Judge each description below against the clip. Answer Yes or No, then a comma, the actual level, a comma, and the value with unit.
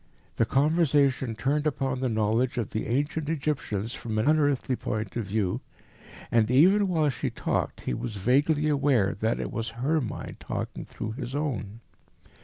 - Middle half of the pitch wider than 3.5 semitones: Yes, average, 4.8 semitones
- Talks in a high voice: No, low, 130 Hz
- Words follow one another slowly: No, average, 165 wpm